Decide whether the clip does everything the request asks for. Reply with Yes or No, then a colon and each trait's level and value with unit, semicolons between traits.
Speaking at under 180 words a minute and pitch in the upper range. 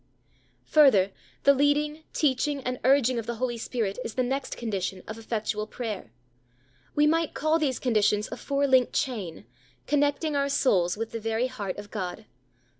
Yes: average, 165 wpm; very high, 250 Hz